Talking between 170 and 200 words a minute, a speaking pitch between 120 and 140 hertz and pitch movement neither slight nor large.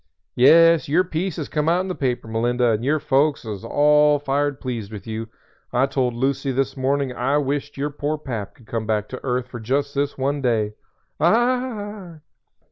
Yes: average, 195 wpm; low, 135 Hz; average, 3.5 semitones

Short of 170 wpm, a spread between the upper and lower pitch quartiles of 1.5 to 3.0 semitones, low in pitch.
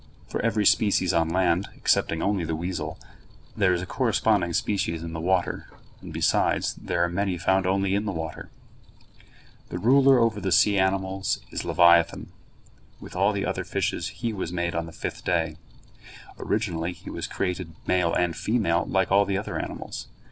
No: average, 175 wpm; average, 2.7 semitones; very low, 95 Hz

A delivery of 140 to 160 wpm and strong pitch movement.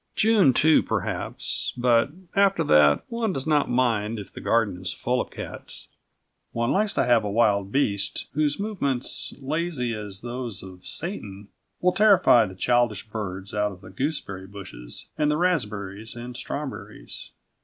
Yes: average, 155 wpm; wide, 6.8 semitones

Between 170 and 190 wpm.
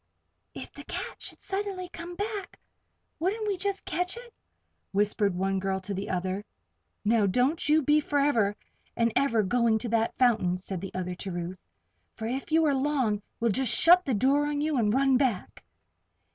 Yes: average, 180 wpm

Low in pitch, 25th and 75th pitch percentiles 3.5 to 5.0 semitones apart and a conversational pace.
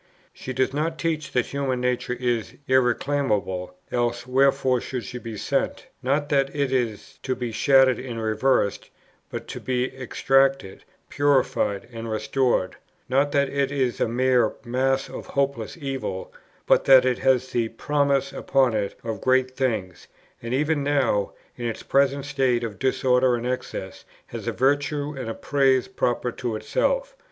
No: low, 130 Hz; narrow, 2.5 semitones; average, 160 wpm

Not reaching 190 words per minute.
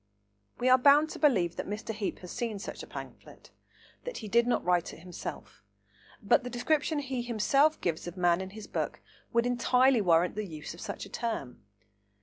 No: average, 200 wpm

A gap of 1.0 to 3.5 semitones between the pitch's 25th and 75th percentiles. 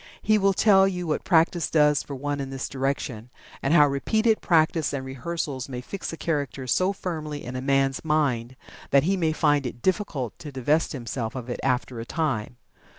No: average, 4.0 semitones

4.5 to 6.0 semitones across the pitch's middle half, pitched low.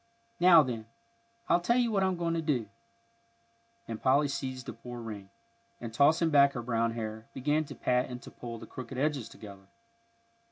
Yes: average, 5.1 semitones; low, 130 Hz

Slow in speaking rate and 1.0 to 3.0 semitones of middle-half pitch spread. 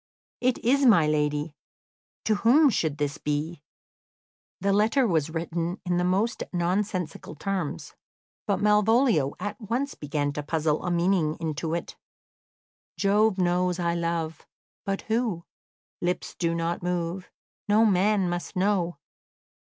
No: slow, 130 wpm; average, 4.3 semitones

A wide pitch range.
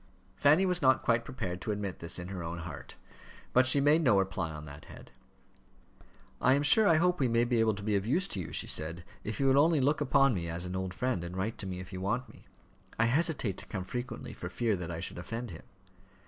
Yes: wide, 6.6 semitones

